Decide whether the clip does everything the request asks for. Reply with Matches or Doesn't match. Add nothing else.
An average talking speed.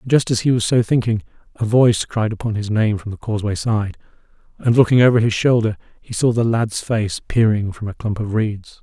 Doesn't match